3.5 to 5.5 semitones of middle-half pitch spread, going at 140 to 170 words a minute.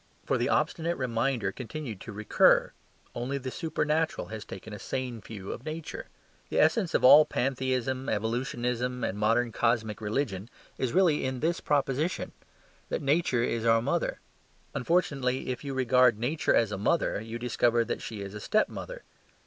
Yes: average, 3.9 semitones; average, 165 wpm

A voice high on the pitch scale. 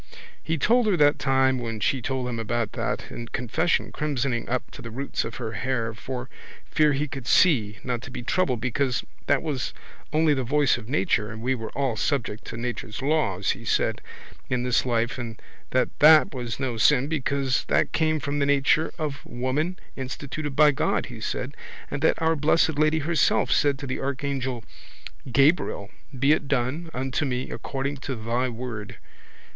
No: low, 130 Hz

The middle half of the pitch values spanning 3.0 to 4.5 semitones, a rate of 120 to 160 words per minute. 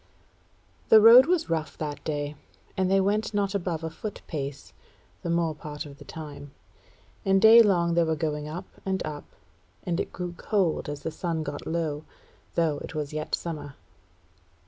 No: average, 4.2 semitones; average, 170 wpm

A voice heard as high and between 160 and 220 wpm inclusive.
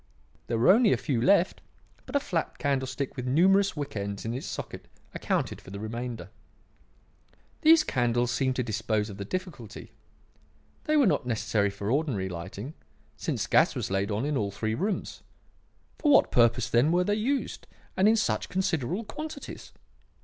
No: low, 130 Hz; average, 170 wpm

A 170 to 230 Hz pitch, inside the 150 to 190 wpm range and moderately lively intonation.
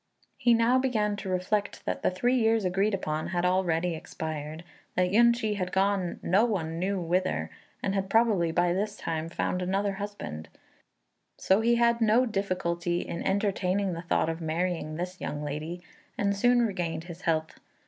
Yes: medium, 185 Hz; average, 170 wpm; average, 3.5 semitones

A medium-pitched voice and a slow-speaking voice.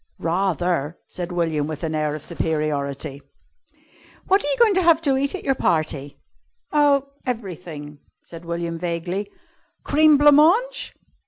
No: medium, 175 Hz; average, 145 wpm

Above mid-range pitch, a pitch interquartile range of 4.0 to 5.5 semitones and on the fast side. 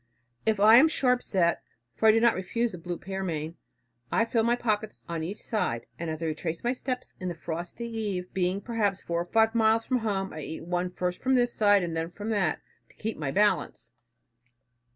Yes: high, 195 Hz; average, 4.8 semitones; fast, 215 wpm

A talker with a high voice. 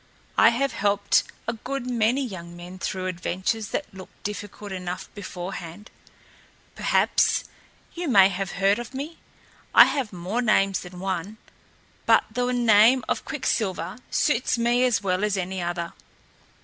Yes: high, 205 Hz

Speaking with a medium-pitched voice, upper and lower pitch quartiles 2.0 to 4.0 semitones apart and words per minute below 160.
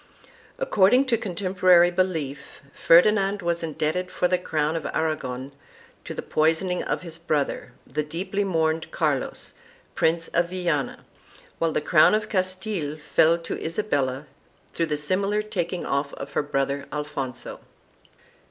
Yes: medium, 165 Hz; average, 3.7 semitones; slow, 135 wpm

